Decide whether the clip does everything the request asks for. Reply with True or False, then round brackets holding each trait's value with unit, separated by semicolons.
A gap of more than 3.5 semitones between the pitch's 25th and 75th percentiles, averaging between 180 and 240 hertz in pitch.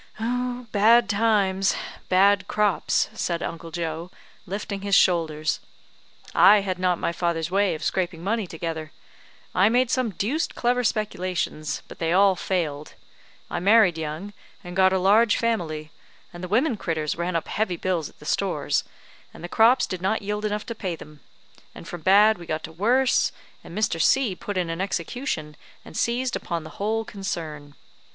True (4.1 semitones; 185 Hz)